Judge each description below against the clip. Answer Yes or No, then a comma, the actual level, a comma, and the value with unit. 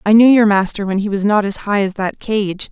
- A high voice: Yes, high, 205 Hz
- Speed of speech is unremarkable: No, fast, 285 wpm